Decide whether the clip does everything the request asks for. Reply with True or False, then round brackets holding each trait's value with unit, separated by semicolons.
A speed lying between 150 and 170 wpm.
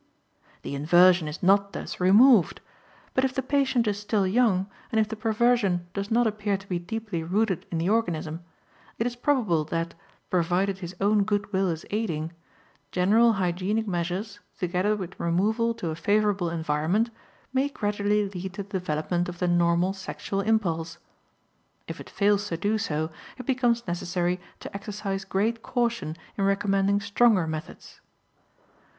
True (155 wpm)